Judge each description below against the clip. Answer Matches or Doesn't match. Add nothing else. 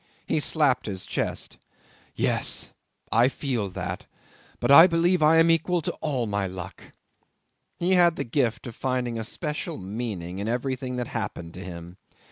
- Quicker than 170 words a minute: Doesn't match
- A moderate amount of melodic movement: Doesn't match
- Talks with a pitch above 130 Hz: Doesn't match